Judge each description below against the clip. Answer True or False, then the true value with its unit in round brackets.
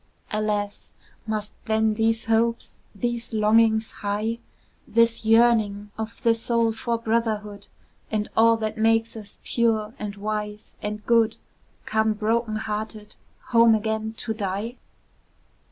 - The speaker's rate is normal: False (120 wpm)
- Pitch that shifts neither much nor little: False (1.3 semitones)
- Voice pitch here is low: False (220 Hz)